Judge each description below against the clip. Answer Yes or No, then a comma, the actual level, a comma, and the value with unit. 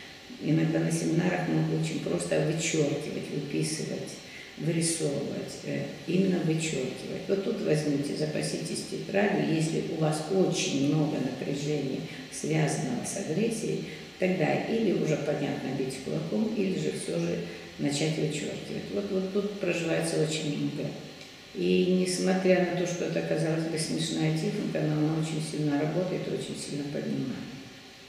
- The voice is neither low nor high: Yes, medium, 155 Hz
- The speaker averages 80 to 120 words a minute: No, average, 130 wpm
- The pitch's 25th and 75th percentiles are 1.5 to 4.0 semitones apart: No, wide, 5.4 semitones